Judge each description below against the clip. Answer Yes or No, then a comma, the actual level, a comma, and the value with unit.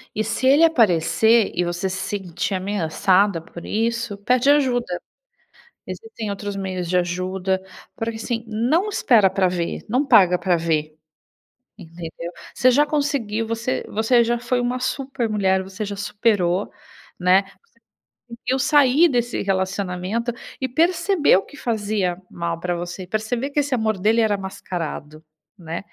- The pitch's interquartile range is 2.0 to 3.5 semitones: No, average, 4.9 semitones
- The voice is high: Yes, high, 210 Hz